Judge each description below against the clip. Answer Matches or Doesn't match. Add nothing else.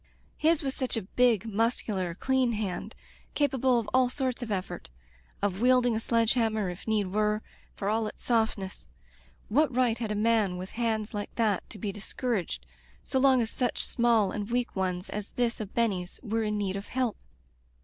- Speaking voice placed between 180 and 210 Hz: Doesn't match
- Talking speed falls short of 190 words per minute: Doesn't match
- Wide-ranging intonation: Doesn't match